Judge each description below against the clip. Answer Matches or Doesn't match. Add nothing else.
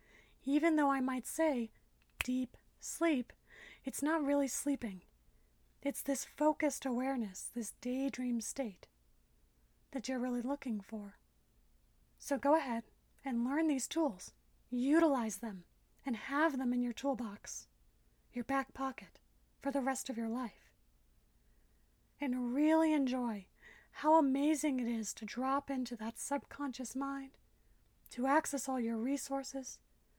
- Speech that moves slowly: Matches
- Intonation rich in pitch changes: Doesn't match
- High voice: Matches